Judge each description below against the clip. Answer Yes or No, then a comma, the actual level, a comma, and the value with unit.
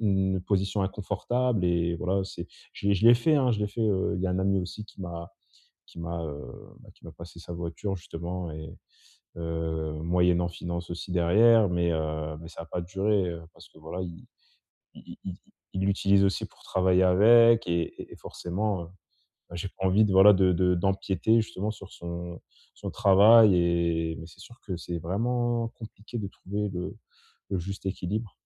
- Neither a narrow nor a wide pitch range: Yes, average, 3.0 semitones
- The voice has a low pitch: Yes, very low, 95 Hz